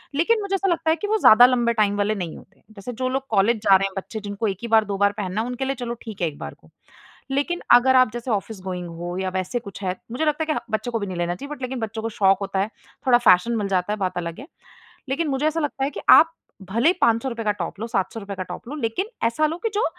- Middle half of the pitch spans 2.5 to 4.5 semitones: No, wide, 5.4 semitones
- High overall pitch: Yes, high, 225 Hz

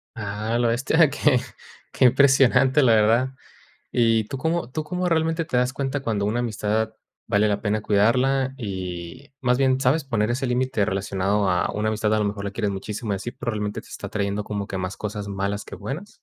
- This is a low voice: Yes, low, 115 Hz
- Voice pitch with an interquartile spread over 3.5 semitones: Yes, average, 4.4 semitones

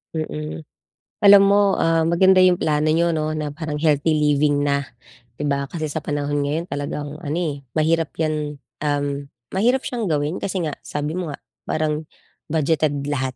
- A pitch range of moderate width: No, narrow, 2.2 semitones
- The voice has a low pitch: No, medium, 155 Hz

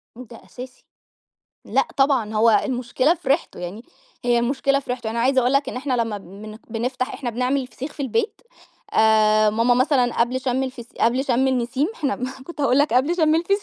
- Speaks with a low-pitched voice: No, very high, 255 Hz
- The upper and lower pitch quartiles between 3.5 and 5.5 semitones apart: No, average, 2.9 semitones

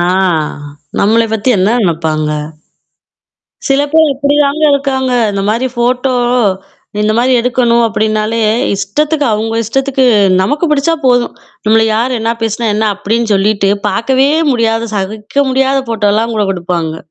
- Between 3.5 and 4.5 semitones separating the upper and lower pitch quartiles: Yes, average, 3.9 semitones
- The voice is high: Yes, high, 230 Hz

